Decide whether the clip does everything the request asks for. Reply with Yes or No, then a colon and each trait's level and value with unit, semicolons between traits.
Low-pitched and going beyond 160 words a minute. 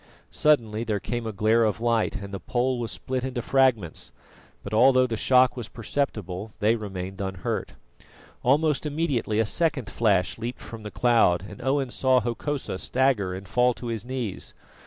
Yes: low, 115 Hz; average, 170 wpm